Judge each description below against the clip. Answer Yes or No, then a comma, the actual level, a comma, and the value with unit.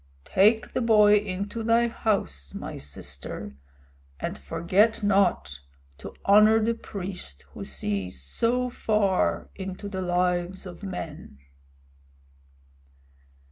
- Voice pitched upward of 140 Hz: Yes, high, 190 Hz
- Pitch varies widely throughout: Yes, wide, 6.4 semitones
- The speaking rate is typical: No, slow, 105 wpm